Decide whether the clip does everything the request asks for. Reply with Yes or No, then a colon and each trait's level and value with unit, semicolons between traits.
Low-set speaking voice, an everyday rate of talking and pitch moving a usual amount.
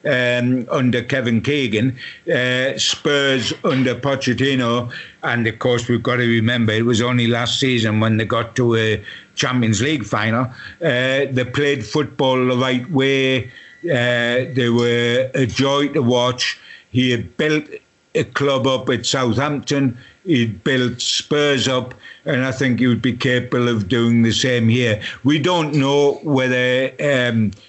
No: low, 125 Hz; average, 155 wpm; narrow, 2.2 semitones